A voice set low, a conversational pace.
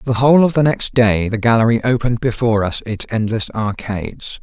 Yes: low, 115 Hz; average, 190 wpm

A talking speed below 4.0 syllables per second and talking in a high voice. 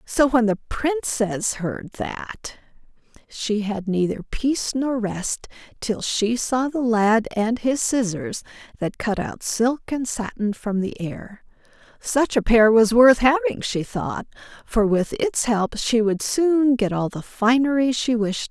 Yes: 3.8 syllables/s; high, 230 Hz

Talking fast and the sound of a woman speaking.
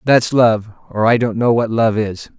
No: fast, 225 wpm; male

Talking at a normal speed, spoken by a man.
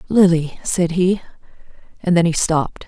No: average, 145 wpm; female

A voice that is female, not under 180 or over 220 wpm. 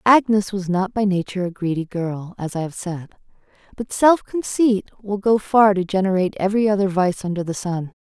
Yes: female; average, 195 wpm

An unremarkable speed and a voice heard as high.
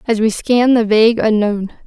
Yes: average, 195 wpm; high, 220 Hz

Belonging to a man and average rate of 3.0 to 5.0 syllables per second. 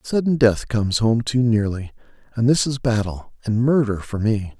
Yes: male; 4.8 syllables/s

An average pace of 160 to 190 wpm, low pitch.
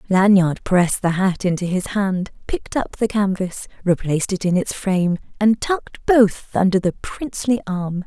No: average, 170 wpm; high, 195 Hz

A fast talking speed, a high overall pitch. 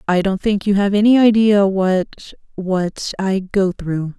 No: average, 160 wpm; high, 195 Hz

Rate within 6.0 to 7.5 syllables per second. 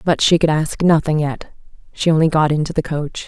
No: 5.4 syllables/s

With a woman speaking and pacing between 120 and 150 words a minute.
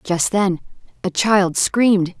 Yes: female; slow, 135 wpm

